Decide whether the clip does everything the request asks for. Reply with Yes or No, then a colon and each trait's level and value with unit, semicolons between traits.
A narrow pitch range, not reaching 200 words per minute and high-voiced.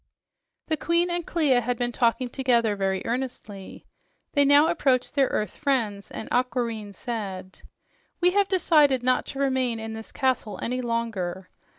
No: average, 3.9 semitones; average, 155 wpm; high, 245 Hz